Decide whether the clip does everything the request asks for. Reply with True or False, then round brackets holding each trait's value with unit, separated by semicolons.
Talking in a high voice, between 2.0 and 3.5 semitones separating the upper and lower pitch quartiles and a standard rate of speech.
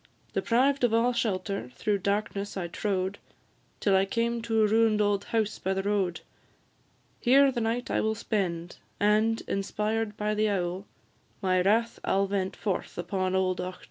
True (205 Hz; 2.8 semitones; 170 wpm)